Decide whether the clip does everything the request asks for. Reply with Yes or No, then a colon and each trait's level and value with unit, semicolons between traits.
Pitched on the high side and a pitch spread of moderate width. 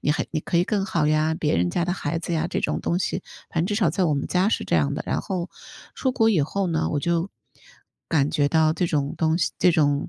No: medium, 165 Hz; average, 3.2 semitones